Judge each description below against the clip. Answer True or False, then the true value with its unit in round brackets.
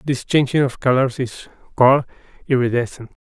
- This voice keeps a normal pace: False (130 wpm)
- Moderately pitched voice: False (130 Hz)